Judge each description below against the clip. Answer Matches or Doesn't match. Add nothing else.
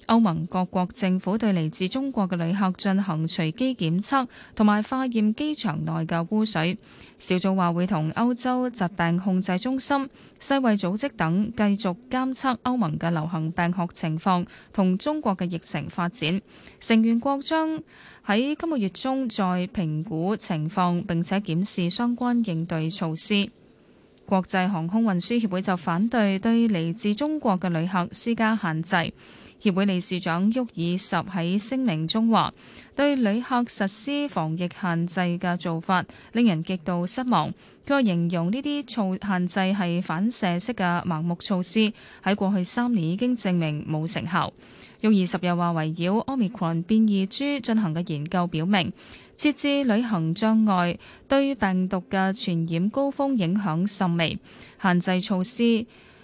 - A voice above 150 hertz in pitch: Matches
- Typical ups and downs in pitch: Matches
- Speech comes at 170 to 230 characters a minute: Doesn't match